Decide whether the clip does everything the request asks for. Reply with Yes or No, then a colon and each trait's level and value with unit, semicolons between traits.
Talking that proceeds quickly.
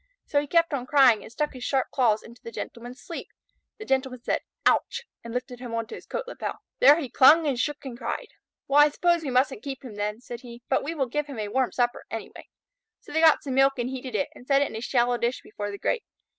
Yes: fast, 255 wpm